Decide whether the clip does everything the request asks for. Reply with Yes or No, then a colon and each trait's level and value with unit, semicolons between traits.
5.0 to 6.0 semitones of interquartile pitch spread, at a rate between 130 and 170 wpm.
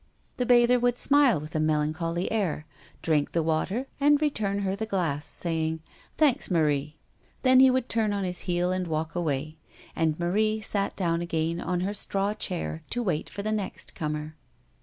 No: average, 5.3 semitones; average, 180 wpm